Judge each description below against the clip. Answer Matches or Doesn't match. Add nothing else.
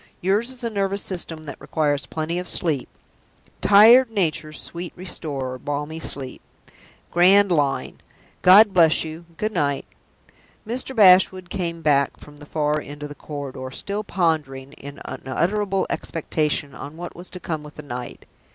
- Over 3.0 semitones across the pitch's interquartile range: Matches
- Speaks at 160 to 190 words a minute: Doesn't match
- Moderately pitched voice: Matches